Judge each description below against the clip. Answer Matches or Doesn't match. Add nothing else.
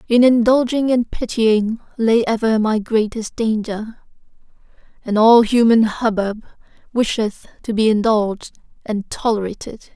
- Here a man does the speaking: Doesn't match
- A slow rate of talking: Matches